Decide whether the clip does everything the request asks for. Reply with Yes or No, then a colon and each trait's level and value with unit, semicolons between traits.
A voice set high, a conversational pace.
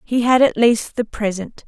No: high, 230 Hz; fast, 215 wpm